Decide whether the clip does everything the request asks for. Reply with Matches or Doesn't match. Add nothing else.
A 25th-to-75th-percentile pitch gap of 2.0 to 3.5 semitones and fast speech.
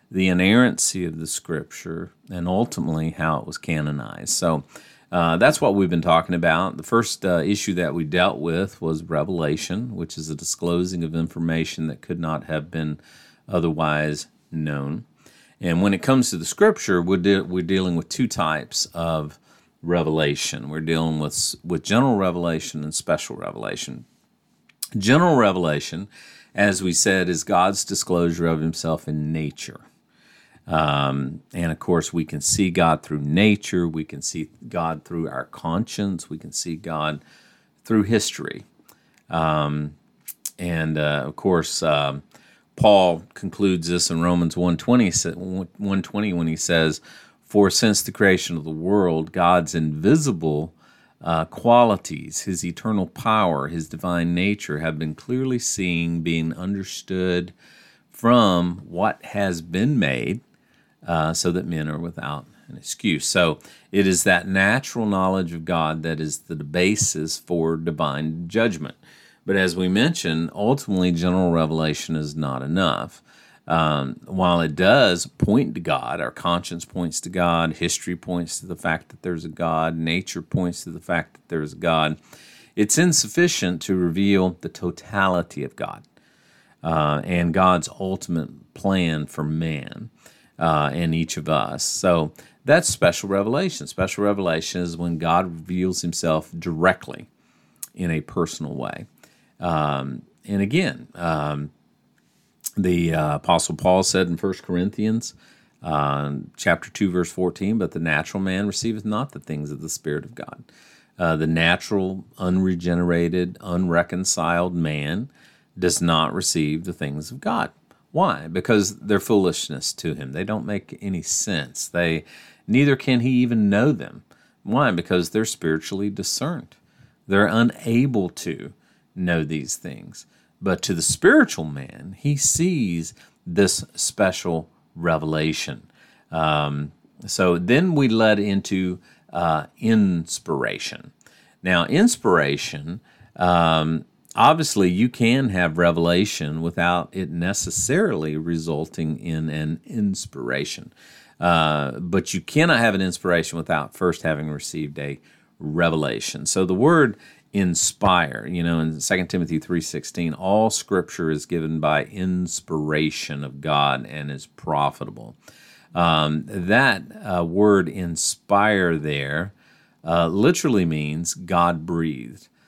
Doesn't match